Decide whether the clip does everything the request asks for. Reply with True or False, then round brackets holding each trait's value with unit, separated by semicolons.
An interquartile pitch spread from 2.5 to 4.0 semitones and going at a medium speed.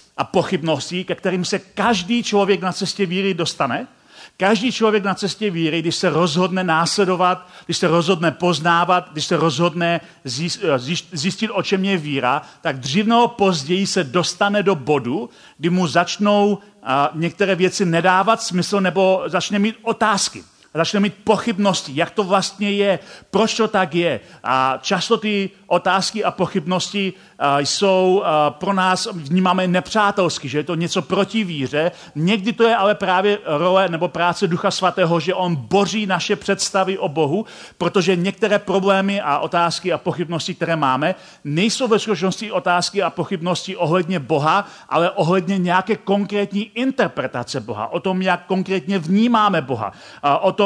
True (2.8 semitones; 150 wpm)